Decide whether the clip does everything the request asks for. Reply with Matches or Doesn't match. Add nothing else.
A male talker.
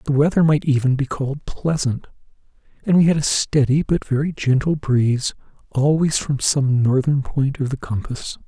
Matches